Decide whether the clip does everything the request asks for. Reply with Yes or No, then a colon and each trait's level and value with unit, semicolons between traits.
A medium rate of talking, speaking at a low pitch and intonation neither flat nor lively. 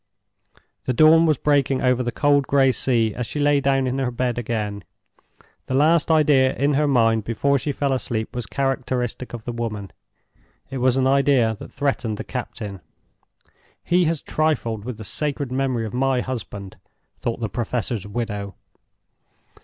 Yes: average, 160 wpm; low, 130 Hz; average, 3.5 semitones